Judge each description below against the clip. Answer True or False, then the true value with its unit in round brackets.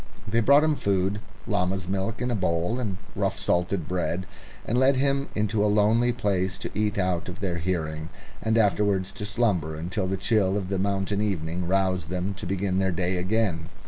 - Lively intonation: False (2.8 semitones)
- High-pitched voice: False (95 Hz)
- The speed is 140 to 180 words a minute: False (190 wpm)